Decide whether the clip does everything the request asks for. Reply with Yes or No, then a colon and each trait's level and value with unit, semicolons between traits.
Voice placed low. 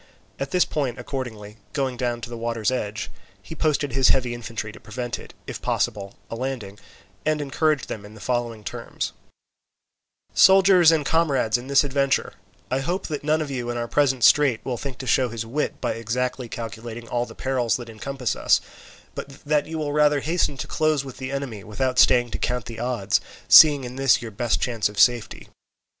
Yes: low, 125 Hz